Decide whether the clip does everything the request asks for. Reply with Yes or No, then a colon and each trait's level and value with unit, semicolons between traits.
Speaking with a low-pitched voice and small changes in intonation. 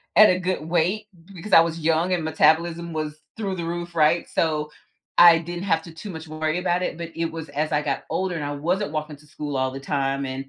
No: medium, 165 Hz; narrow, 2.3 semitones